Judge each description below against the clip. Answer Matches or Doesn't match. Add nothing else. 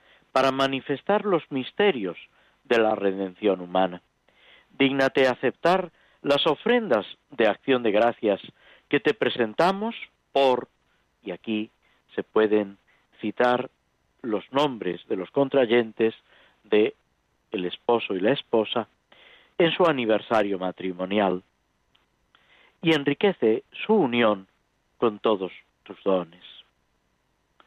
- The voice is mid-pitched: Doesn't match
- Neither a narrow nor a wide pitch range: Doesn't match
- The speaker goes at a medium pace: Doesn't match